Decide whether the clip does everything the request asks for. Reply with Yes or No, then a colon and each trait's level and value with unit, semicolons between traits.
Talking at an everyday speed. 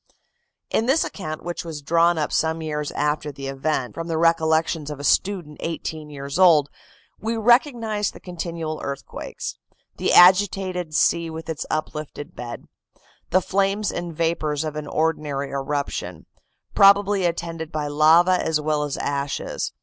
Yes: average, 150 wpm